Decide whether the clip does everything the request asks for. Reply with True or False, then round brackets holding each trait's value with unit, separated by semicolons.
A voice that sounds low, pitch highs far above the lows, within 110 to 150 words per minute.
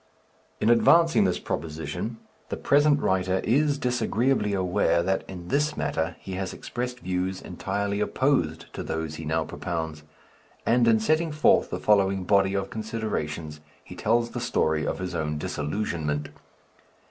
True (95 Hz; 6.3 semitones; 145 wpm)